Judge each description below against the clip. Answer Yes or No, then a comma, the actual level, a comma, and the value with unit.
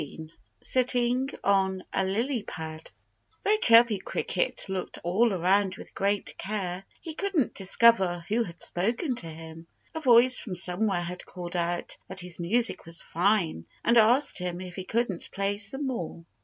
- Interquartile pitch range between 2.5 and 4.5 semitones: No, average, 5.1 semitones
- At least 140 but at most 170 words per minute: Yes, average, 160 wpm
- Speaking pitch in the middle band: No, high, 195 Hz